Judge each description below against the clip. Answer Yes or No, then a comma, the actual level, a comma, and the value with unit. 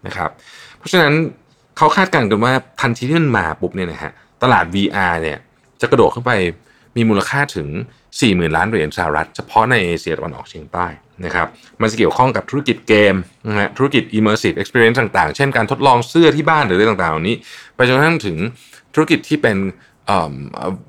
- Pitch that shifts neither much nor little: No, wide, 6.6 semitones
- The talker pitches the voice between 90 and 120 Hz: Yes, low, 115 Hz